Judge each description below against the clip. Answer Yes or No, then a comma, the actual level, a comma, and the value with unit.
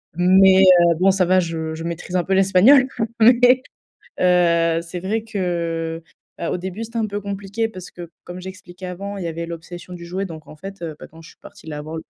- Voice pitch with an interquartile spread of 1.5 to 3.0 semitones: Yes, narrow, 2.6 semitones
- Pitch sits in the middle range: Yes, medium, 180 Hz